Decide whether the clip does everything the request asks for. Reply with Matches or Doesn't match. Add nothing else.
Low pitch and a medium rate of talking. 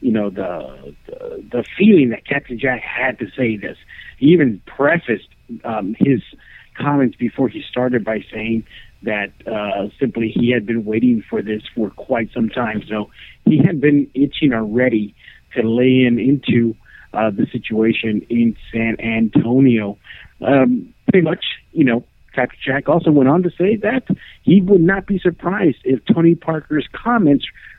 Matches